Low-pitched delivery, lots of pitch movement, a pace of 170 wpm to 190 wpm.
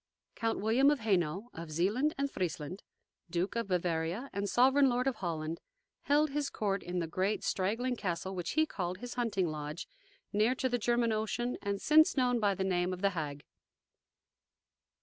No: high, 200 Hz; wide, 5.7 semitones; average, 175 wpm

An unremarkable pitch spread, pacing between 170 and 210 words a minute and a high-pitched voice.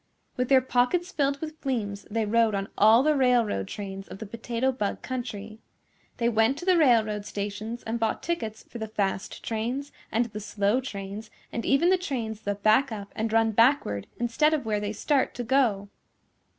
Yes: average, 3.9 semitones; average, 190 wpm; high, 225 Hz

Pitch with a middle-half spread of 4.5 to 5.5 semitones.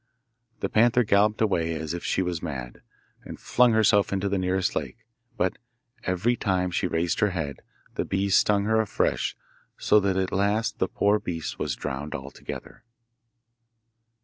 No: average, 3.4 semitones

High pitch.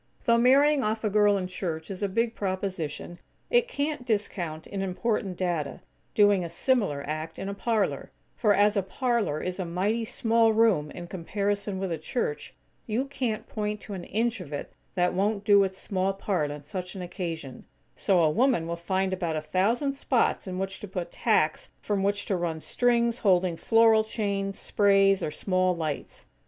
Yes: high, 195 Hz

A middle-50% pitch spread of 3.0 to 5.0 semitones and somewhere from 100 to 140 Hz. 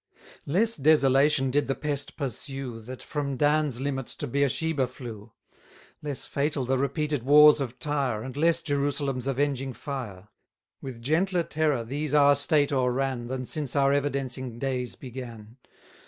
No: narrow, 2.4 semitones; low, 135 Hz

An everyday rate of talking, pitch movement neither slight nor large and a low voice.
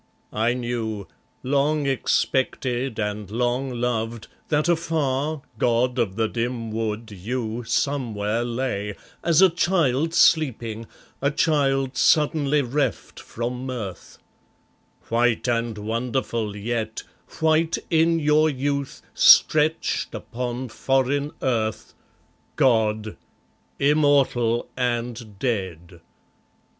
No: slow, 95 wpm; average, 3.9 semitones; low, 125 Hz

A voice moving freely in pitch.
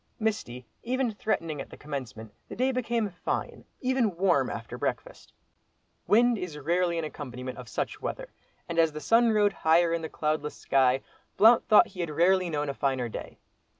Yes: wide, 6.8 semitones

